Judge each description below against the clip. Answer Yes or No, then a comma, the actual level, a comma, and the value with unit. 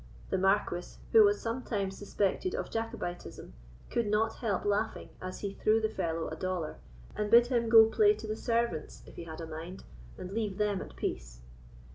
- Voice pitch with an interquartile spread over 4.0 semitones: No, average, 3.7 semitones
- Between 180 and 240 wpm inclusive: Yes, average, 185 wpm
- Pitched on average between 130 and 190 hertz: No, high, 205 Hz